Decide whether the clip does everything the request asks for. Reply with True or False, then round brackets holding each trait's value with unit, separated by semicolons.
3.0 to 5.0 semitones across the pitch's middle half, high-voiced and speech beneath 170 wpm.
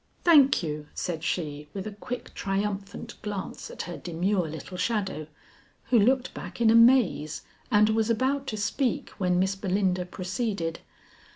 True (4.4 semitones; 200 Hz; 150 wpm)